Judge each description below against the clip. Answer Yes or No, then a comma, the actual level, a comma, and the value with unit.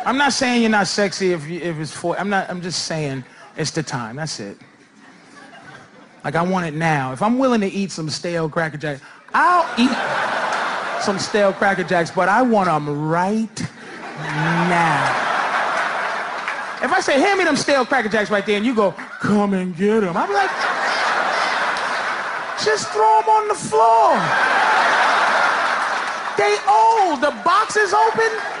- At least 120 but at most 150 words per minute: No, average, 165 wpm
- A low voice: No, high, 205 Hz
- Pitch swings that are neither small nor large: No, wide, 8.0 semitones